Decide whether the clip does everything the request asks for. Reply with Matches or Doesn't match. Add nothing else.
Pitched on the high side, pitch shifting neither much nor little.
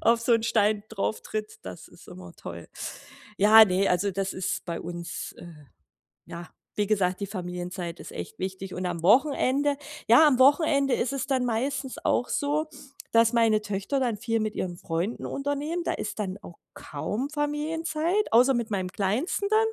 Doesn't match